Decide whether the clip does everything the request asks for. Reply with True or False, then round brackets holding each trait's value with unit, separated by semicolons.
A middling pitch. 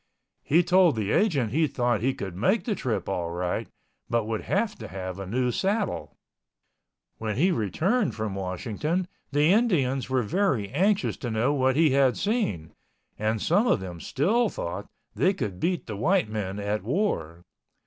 False (125 Hz)